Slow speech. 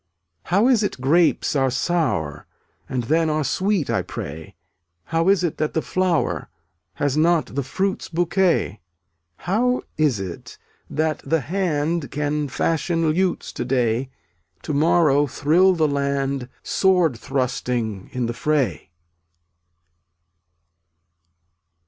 Yes: slow, 125 wpm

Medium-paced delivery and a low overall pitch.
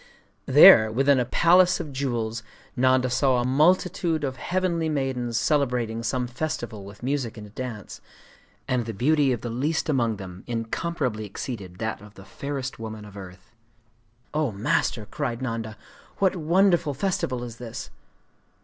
Yes: average, 150 wpm; low, 125 Hz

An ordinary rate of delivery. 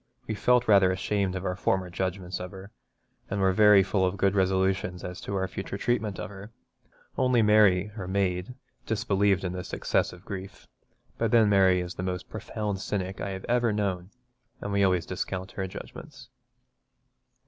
Yes: average, 175 wpm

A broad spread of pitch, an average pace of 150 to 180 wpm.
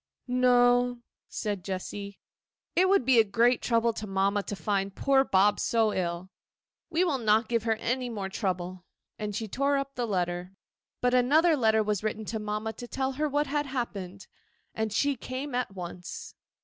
No: average, 4.1 semitones; average, 175 wpm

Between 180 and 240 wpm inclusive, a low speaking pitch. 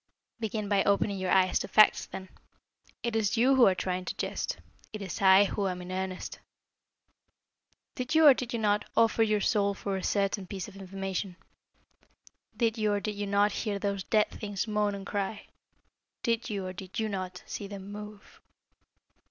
No: average, 185 wpm; high, 200 Hz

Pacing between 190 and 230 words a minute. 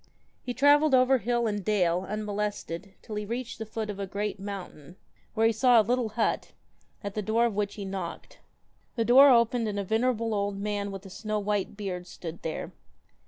Yes: average, 200 wpm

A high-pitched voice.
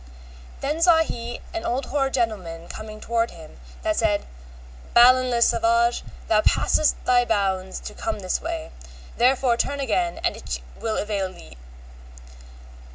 Yes: high, 235 Hz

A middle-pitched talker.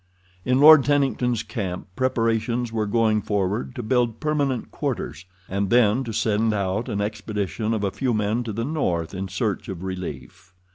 No: low, 110 Hz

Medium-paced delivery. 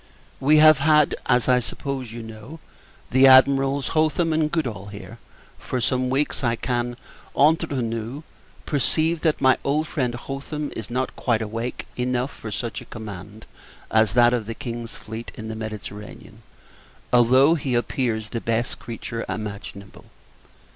Yes: average, 150 wpm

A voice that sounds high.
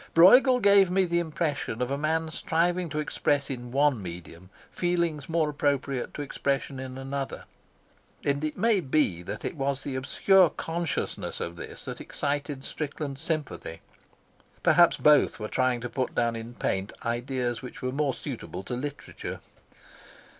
No: medium, 140 Hz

